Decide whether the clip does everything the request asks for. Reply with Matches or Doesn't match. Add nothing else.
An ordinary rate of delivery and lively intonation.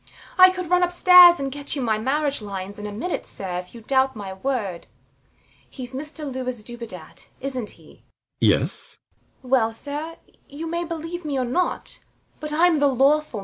Matches